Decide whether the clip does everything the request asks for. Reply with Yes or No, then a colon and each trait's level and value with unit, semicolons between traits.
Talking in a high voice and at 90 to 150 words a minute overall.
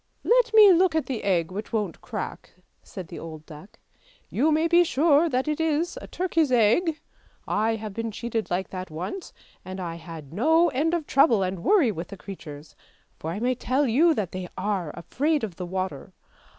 No: high, 225 Hz; fast, 205 wpm